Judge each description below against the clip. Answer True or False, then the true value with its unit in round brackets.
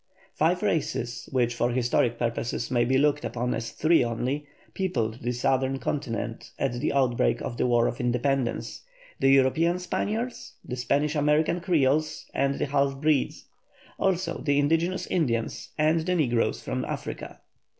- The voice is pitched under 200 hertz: True (135 Hz)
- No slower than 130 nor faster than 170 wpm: True (150 wpm)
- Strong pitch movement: False (4.4 semitones)